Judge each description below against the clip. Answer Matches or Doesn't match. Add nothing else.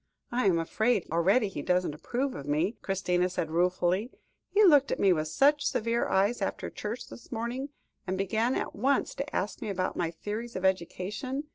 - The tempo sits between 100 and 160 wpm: Doesn't match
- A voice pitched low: Doesn't match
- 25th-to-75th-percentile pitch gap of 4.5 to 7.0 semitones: Matches